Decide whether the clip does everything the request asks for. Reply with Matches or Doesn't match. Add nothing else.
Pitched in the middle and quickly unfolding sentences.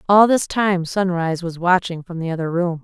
Matches